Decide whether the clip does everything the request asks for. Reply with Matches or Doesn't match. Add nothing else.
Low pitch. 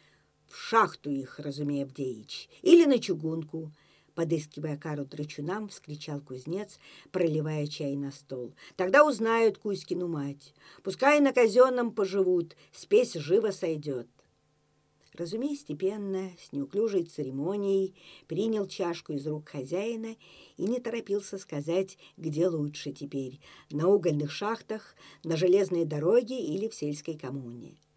Doesn't match